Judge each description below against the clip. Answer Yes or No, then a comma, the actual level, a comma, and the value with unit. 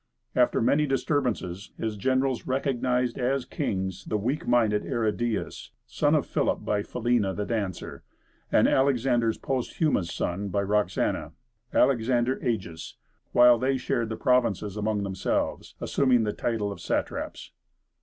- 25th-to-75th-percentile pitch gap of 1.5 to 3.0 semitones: No, average, 3.9 semitones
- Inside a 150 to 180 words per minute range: No, slow, 135 wpm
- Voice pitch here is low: Yes, low, 115 Hz